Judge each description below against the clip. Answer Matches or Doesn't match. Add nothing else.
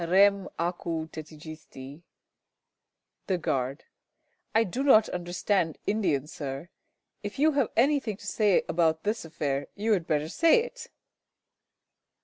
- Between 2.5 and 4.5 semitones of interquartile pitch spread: Doesn't match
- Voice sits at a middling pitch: Matches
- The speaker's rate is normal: Doesn't match